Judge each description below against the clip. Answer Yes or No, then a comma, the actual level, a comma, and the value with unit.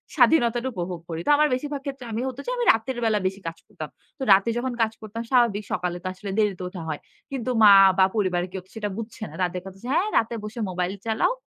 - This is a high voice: Yes, high, 220 Hz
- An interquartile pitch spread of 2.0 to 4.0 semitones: No, average, 4.4 semitones